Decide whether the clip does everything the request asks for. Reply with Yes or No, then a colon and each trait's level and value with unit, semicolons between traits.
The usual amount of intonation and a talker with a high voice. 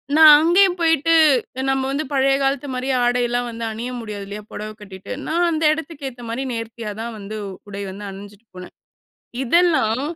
No: wide, 5.9 semitones; high, 245 Hz